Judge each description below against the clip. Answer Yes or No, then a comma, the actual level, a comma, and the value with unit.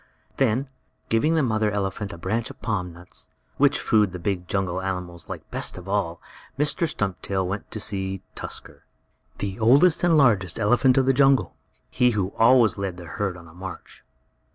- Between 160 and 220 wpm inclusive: Yes, average, 175 wpm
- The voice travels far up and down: No, average, 4.7 semitones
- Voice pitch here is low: Yes, low, 100 Hz